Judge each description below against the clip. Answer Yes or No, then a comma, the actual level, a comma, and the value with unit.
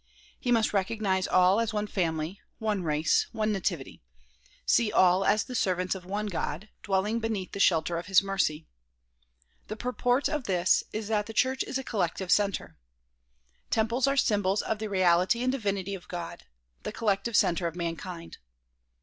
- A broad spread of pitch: No, average, 3.4 semitones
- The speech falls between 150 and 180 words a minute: Yes, average, 165 wpm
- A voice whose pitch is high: Yes, high, 200 Hz